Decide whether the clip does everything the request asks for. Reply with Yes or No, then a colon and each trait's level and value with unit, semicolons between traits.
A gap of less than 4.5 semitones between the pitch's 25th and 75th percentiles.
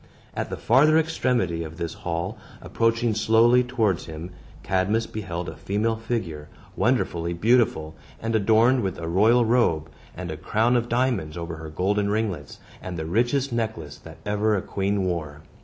No: wide, 5.4 semitones